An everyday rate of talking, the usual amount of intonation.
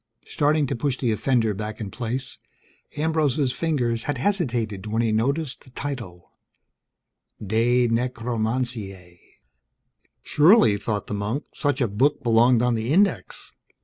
No: slow, 130 wpm; average, 4.1 semitones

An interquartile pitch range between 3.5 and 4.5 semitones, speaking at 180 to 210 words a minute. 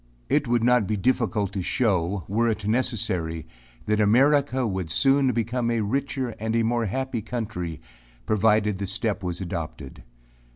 No: average, 3.9 semitones; average, 150 wpm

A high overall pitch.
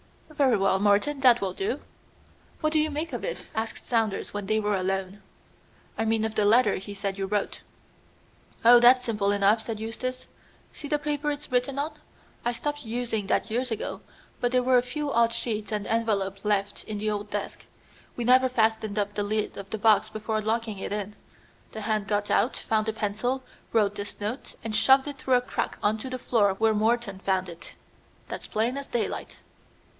Yes: high, 220 Hz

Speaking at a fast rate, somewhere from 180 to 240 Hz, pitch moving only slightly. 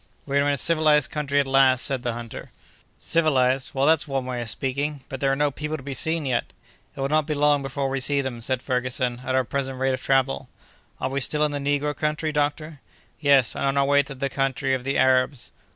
No: fast, 240 wpm; low, 135 Hz; narrow, 1.9 semitones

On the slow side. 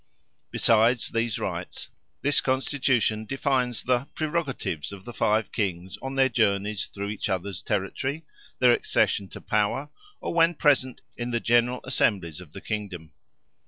No: average, 145 wpm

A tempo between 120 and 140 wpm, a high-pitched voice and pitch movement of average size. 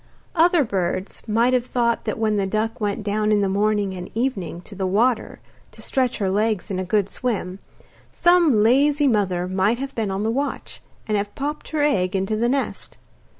No: average, 195 wpm; high, 215 Hz; average, 4.4 semitones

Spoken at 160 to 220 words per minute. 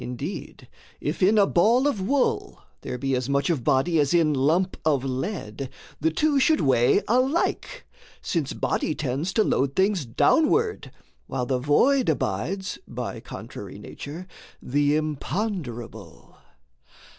No: slow, 135 wpm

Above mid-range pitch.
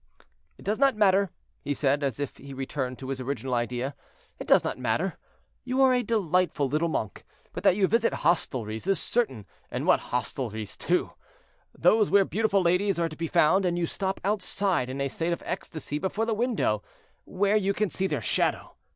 No: medium, 170 Hz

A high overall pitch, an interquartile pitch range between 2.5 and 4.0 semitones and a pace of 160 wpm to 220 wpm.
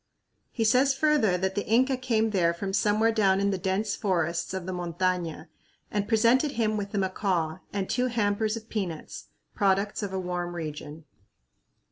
Yes: high, 200 Hz; average, 3.6 semitones; average, 170 wpm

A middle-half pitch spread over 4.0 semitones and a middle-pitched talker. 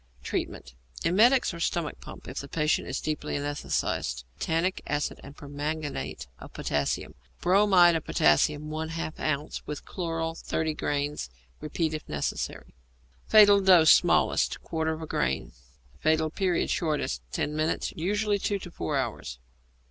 No: average, 2.9 semitones; medium, 155 Hz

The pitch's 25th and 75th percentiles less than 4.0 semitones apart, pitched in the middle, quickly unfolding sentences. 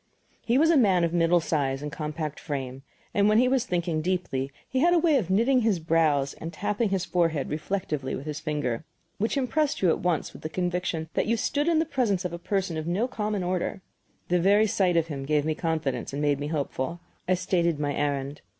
No: wide, 5.4 semitones; medium, 175 Hz; fast, 225 wpm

